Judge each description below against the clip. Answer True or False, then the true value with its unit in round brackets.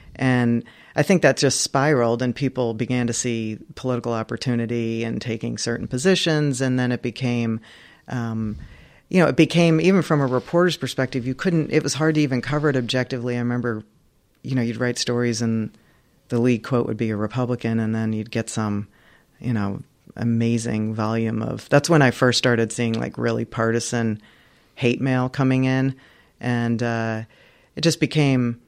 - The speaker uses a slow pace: False (175 wpm)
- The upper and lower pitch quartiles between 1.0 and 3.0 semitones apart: True (2.5 semitones)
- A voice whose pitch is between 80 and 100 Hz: False (120 Hz)